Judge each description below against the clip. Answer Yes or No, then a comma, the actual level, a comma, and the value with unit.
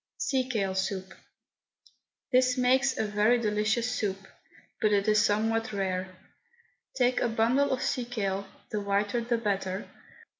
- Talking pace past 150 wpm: No, average, 140 wpm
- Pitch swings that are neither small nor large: Yes, average, 3.6 semitones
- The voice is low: No, high, 215 Hz